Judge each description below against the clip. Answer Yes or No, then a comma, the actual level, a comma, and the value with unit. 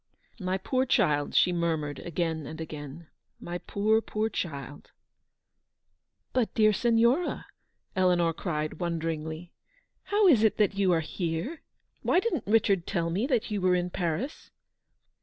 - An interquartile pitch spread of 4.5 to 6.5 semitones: Yes, average, 5.3 semitones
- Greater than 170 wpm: No, average, 160 wpm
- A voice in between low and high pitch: Yes, medium, 180 Hz